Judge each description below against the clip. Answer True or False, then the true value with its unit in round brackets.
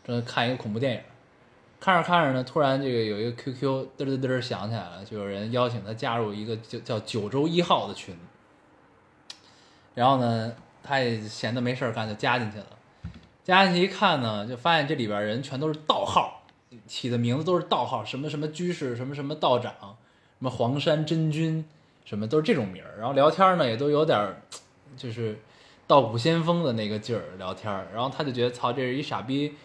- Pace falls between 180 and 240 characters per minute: False (305 characters per minute)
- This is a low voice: True (125 Hz)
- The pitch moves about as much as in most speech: True (4.8 semitones)